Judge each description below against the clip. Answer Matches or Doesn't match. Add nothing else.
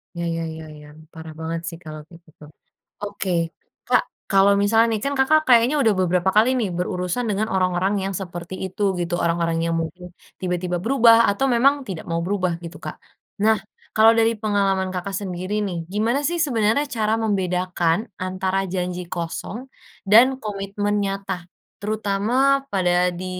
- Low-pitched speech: Doesn't match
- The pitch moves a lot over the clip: Doesn't match